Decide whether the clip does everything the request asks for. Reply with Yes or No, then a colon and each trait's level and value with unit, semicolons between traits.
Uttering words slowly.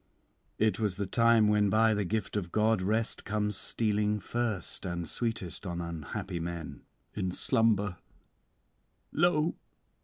Yes: slow, 130 wpm